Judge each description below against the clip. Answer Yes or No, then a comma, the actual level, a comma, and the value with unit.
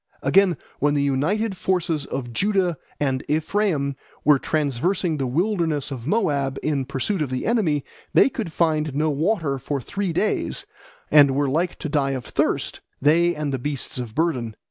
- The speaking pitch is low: No, medium, 150 Hz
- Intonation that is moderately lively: Yes, average, 4.2 semitones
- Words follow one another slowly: No, average, 165 wpm